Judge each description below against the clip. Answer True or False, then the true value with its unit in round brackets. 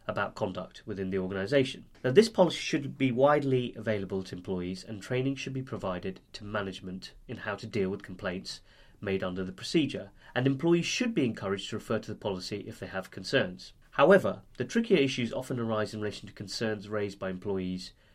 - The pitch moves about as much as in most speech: False (5.7 semitones)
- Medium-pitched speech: False (110 Hz)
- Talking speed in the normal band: True (190 wpm)